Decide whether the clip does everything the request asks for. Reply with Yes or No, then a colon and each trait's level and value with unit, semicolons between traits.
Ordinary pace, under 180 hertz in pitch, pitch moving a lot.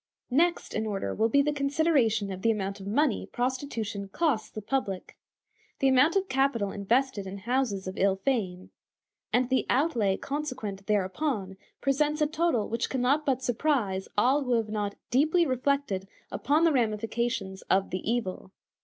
No: average, 160 wpm; high, 240 Hz; wide, 5.7 semitones